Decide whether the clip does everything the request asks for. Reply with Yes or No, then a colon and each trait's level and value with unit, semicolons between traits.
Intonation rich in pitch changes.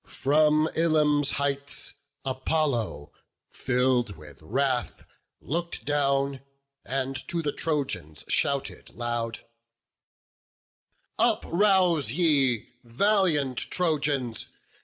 No: average, 3.7 semitones